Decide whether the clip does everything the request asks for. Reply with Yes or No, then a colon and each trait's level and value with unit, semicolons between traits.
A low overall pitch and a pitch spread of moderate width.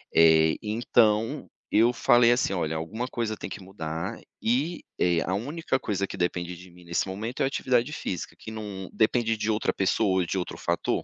Yes: low, 105 Hz; average, 5.0 semitones